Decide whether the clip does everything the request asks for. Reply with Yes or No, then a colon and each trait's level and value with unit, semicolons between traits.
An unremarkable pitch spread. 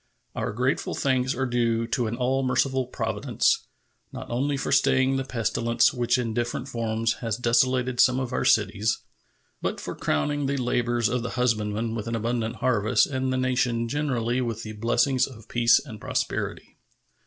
No: narrow, 2.1 semitones